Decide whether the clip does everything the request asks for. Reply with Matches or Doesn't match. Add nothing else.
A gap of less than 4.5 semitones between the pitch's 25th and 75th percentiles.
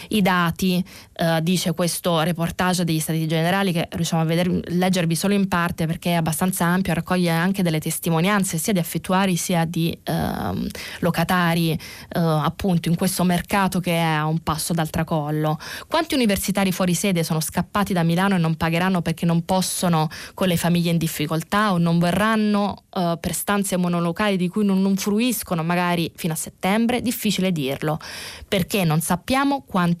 Matches